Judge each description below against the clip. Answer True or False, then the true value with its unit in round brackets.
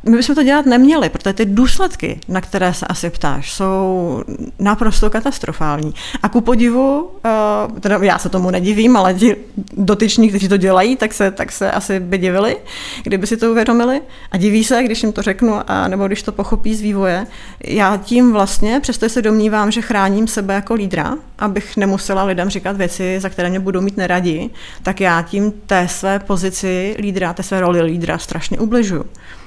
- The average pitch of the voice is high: True (205 Hz)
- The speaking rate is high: True (185 wpm)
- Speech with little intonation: False (3.2 semitones)